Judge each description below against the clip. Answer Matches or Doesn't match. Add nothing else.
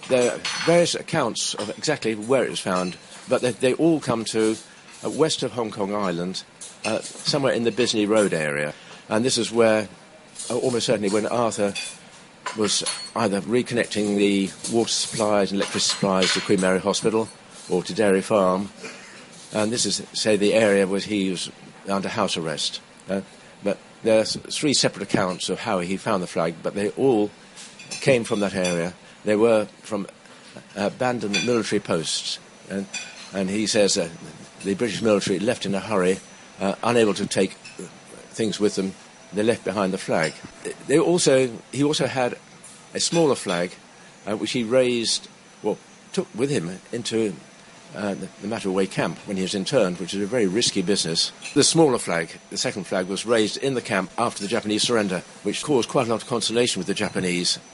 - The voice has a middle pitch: Doesn't match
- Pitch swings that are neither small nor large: Matches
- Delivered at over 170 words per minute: Matches